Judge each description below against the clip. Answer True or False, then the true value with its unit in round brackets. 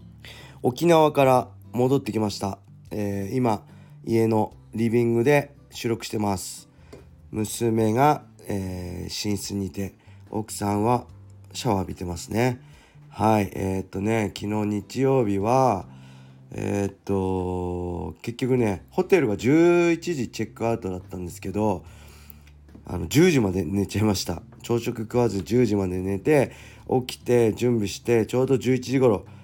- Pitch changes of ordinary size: True (3.9 semitones)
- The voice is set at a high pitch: False (105 Hz)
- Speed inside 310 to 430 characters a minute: False (255 characters per minute)